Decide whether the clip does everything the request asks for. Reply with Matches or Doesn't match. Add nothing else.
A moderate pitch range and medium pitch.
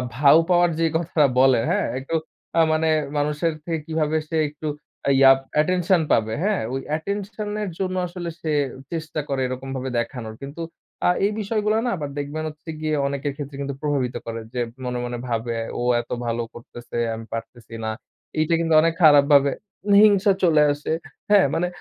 Matches